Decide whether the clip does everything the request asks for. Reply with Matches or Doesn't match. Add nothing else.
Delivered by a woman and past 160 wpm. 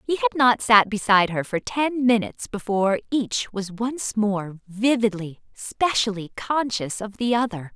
Doesn't match